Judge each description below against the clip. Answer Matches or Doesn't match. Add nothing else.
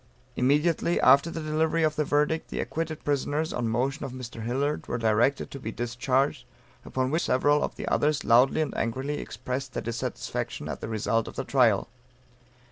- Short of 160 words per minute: Doesn't match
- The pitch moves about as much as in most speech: Matches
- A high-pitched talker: Doesn't match